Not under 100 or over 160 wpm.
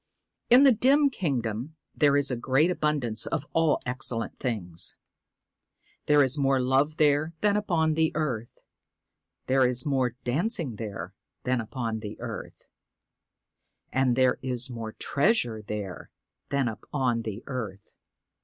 Yes: slow, 135 wpm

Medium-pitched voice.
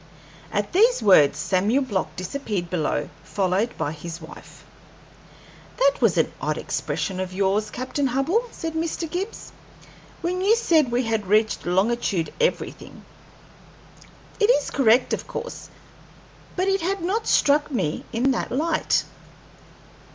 No: high, 245 Hz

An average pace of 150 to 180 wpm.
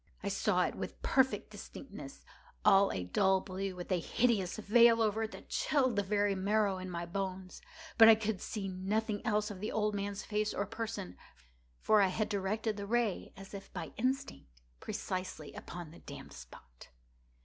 Yes: average, 175 wpm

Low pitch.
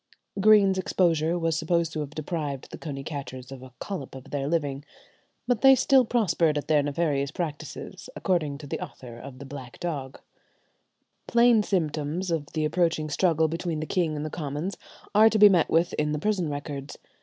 No: medium, 155 Hz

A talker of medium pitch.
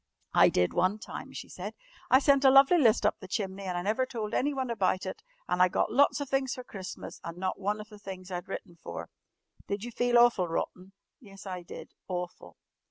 No: high, 205 Hz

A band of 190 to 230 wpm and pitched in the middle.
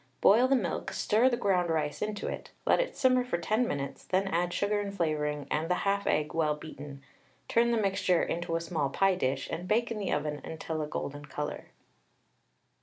Yes: average, 200 wpm; medium, 175 Hz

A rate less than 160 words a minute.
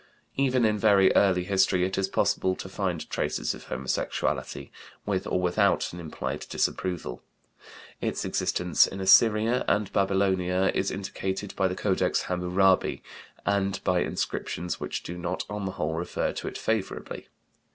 Yes: average, 150 wpm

